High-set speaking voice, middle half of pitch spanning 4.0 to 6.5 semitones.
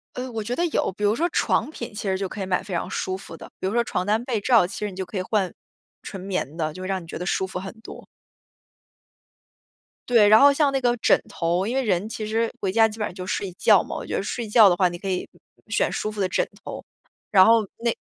No: high, 205 Hz; average, 3.5 semitones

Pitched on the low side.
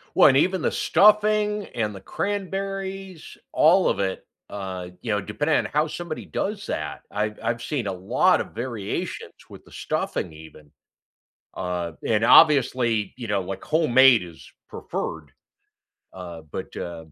Yes: low, 120 Hz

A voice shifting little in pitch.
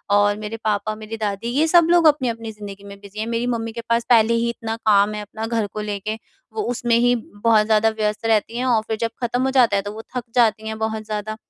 Yes: narrow, 1.8 semitones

